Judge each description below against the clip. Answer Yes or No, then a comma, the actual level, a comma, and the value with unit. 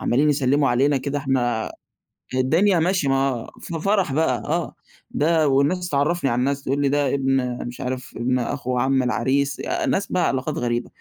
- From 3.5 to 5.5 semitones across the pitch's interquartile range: No, average, 2.7 semitones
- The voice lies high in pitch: No, low, 135 Hz